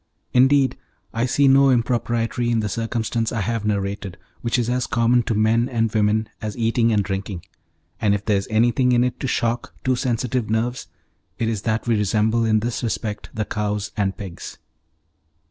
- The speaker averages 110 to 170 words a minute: No, average, 180 wpm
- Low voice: Yes, low, 115 Hz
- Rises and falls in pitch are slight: Yes, narrow, 2.3 semitones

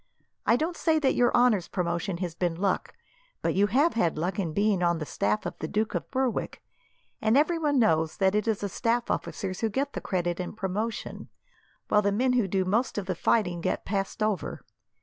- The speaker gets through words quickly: Yes, fast, 210 wpm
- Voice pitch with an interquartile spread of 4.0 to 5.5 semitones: Yes, average, 4.9 semitones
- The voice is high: Yes, high, 205 Hz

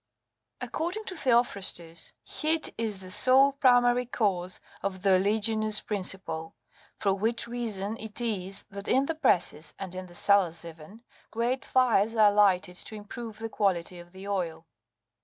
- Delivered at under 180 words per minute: Yes, average, 150 wpm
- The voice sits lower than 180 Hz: No, high, 205 Hz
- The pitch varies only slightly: No, average, 4.2 semitones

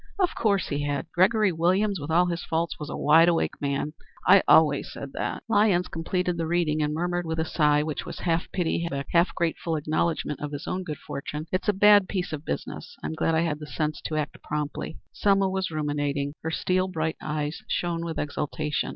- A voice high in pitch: No, medium, 160 Hz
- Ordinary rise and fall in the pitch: Yes, average, 3.1 semitones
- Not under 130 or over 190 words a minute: No, fast, 205 wpm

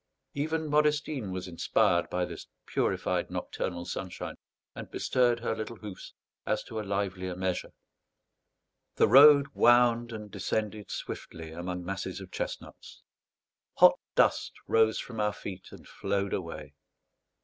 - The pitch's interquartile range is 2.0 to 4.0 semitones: No, average, 4.6 semitones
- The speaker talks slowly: Yes, slow, 130 wpm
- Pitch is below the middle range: Yes, low, 105 Hz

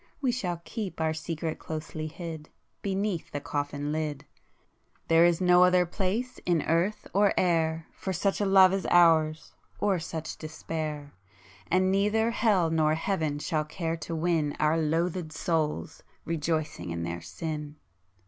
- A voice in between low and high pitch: Yes, medium, 165 Hz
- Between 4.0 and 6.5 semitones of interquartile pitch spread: No, average, 3.0 semitones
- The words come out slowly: No, average, 155 wpm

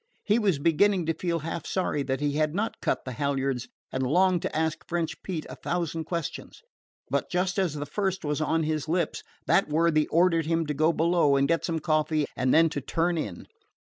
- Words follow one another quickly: Yes, fast, 210 wpm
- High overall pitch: No, medium, 160 Hz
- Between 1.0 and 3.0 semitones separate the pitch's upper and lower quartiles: Yes, average, 2.7 semitones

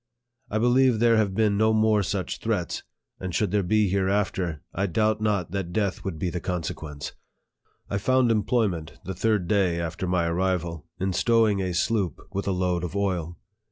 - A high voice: No, very low, 95 Hz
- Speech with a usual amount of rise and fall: Yes, average, 3.4 semitones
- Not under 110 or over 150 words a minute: No, average, 185 wpm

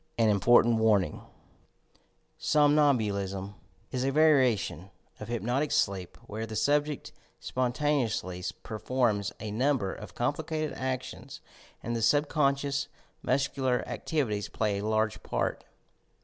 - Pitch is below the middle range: Yes, low, 120 Hz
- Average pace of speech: No, slow, 115 wpm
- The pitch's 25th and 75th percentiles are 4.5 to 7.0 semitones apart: Yes, average, 4.9 semitones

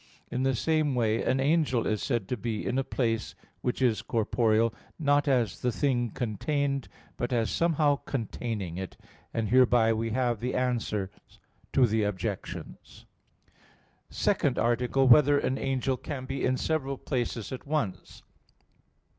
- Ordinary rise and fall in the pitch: Yes, average, 3.1 semitones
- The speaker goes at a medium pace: Yes, average, 165 wpm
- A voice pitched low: Yes, low, 125 Hz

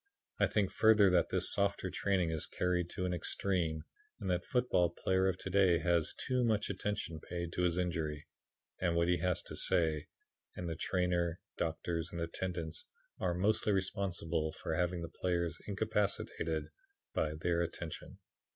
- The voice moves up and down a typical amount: No, narrow, 2.2 semitones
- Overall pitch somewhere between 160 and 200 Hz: No, very low, 90 Hz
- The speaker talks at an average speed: Yes, average, 165 wpm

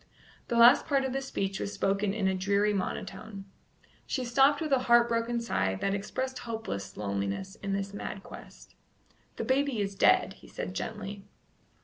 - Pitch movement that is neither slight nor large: Yes, average, 3.6 semitones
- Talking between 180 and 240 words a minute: No, average, 170 wpm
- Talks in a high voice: Yes, high, 210 Hz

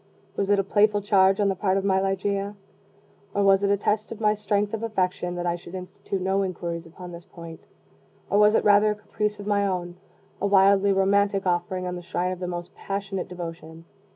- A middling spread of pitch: No, narrow, 2.1 semitones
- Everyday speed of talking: No, fast, 215 wpm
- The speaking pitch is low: No, high, 195 Hz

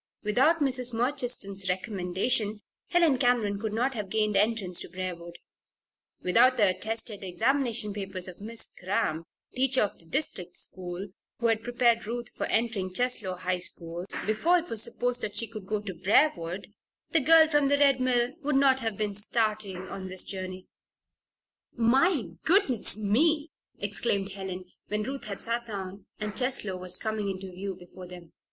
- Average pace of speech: Yes, average, 160 wpm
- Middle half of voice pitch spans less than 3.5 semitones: No, average, 4.7 semitones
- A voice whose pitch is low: No, high, 215 Hz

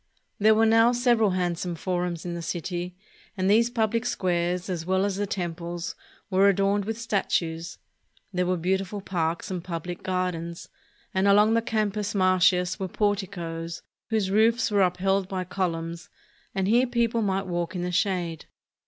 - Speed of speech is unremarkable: Yes, average, 160 wpm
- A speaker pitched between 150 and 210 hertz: Yes, medium, 185 Hz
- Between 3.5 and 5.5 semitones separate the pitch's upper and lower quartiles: No, average, 2.9 semitones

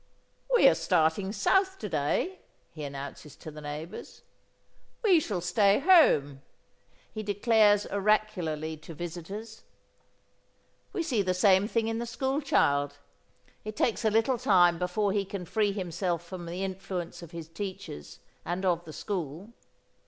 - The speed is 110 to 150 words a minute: Yes, average, 145 wpm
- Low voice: No, high, 190 Hz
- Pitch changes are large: No, average, 4.4 semitones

